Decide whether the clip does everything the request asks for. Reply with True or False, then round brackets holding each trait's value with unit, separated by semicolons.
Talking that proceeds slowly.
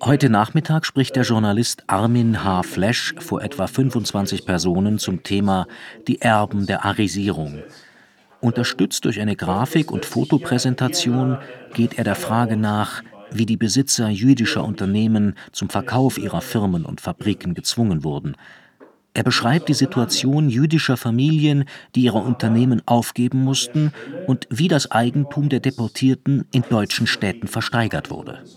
False (135 wpm)